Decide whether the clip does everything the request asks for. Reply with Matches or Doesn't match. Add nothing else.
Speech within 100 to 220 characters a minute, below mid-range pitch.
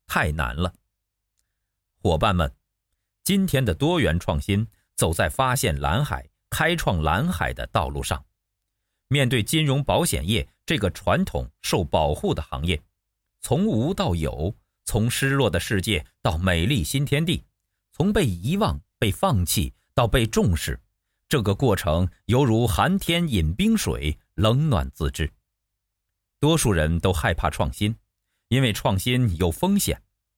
Matches